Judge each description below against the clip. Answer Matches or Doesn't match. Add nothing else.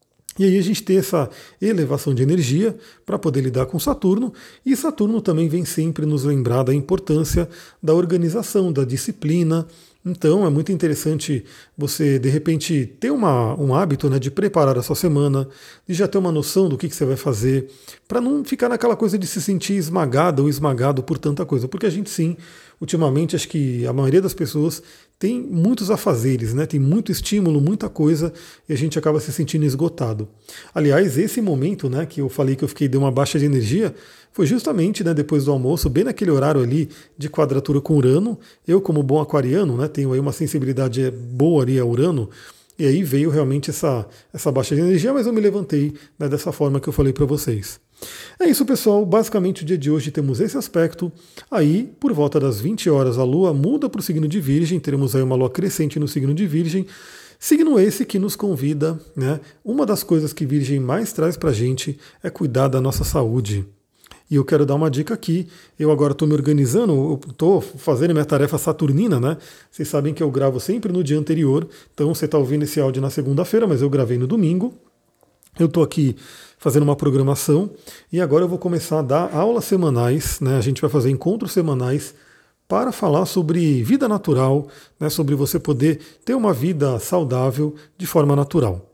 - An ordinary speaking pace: Doesn't match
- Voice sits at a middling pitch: Matches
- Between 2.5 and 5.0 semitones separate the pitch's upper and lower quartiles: Matches